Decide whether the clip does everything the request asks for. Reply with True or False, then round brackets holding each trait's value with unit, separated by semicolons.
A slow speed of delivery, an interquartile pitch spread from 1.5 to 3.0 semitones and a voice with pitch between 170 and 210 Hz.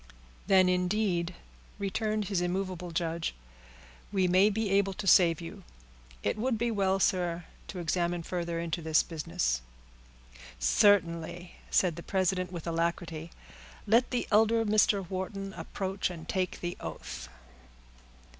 True (130 wpm; 2.7 semitones; 185 Hz)